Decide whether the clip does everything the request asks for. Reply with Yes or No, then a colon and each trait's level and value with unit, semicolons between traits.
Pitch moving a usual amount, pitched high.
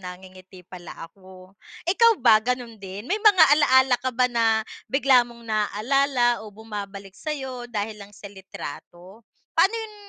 Yes: average, 4.9 semitones; high, 225 Hz